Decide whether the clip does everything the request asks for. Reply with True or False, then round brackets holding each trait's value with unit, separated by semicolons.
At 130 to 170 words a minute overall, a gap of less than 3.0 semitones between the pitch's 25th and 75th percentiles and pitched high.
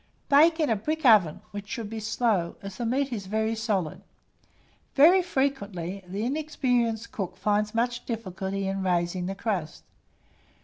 False (150 wpm; 4.3 semitones; 215 Hz)